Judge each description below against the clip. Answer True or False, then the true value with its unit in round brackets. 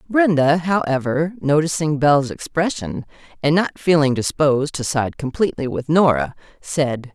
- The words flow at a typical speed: False (125 wpm)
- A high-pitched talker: False (150 Hz)